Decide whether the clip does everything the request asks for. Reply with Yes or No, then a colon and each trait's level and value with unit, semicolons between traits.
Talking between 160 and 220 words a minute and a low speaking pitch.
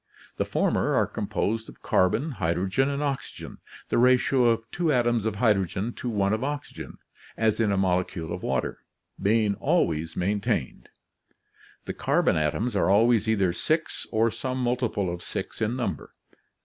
Yes: average, 170 wpm; low, 110 Hz